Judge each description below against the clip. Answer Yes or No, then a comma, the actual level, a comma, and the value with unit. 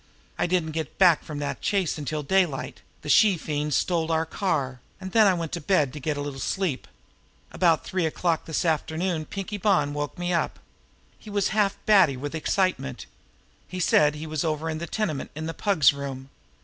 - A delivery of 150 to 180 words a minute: No, average, 195 wpm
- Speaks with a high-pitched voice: No, medium, 160 Hz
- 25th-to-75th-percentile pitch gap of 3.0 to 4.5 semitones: Yes, average, 4.0 semitones